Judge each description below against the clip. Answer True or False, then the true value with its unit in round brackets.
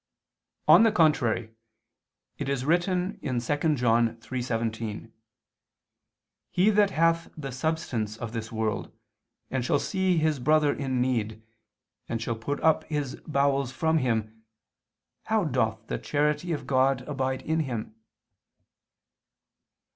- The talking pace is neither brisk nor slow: False (125 wpm)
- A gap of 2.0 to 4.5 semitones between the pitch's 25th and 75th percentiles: False (5.3 semitones)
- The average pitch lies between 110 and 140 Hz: True (135 Hz)